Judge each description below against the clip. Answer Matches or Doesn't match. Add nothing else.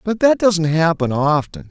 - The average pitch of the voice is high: Doesn't match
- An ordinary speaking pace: Matches